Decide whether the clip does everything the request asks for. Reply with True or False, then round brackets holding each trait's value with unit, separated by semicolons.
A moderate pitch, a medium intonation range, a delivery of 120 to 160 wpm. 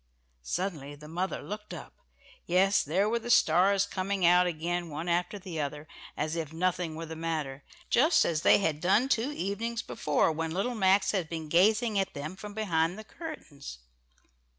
False (180 Hz; 4.1 semitones; 175 wpm)